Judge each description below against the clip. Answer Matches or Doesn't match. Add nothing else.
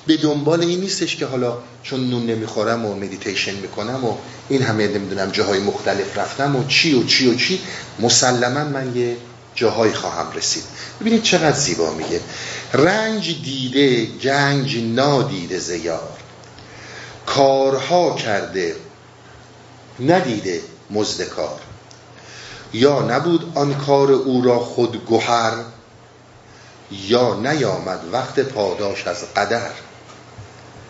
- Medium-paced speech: Matches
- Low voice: Matches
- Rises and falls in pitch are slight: Doesn't match